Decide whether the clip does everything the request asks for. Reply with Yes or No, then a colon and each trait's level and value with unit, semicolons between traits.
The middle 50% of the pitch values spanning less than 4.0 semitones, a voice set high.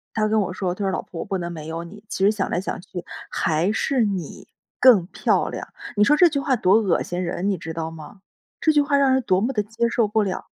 No: average, 4.3 semitones; high, 200 Hz